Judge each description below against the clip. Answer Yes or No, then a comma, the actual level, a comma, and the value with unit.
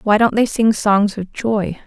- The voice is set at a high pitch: Yes, high, 210 Hz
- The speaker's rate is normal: No, fast, 225 wpm